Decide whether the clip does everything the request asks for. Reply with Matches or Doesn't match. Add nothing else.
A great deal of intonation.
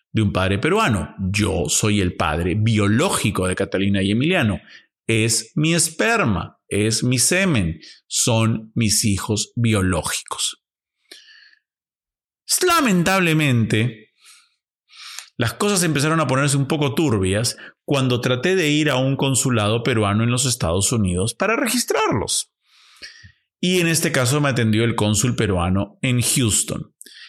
Matches